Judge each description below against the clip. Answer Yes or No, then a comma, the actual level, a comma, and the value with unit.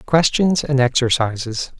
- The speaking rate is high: No, slow, 100 wpm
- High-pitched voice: No, low, 135 Hz